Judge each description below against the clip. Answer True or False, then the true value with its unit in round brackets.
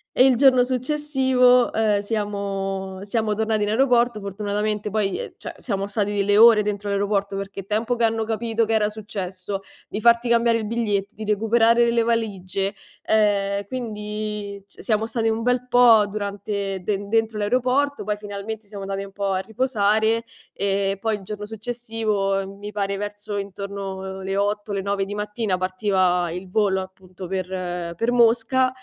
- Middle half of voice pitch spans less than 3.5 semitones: True (2.4 semitones)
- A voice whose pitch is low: False (210 Hz)